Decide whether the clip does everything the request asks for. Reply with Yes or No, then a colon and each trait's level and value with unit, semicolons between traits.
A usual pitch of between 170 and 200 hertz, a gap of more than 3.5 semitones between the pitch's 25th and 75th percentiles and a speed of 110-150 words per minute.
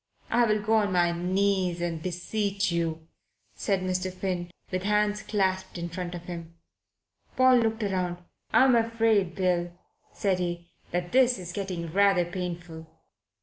No: medium, 185 Hz; average, 2.9 semitones; average, 145 wpm